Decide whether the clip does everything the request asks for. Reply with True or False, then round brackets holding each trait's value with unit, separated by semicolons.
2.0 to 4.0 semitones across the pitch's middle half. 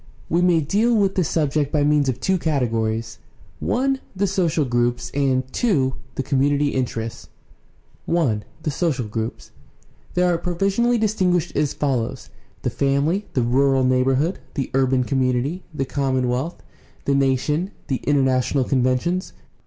False (5.1 semitones)